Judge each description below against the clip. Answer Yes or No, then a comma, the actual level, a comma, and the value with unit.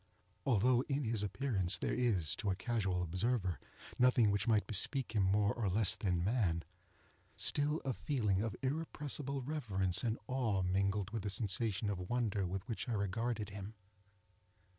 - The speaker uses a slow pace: No, average, 160 wpm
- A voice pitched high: No, low, 105 Hz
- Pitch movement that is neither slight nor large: Yes, average, 4.2 semitones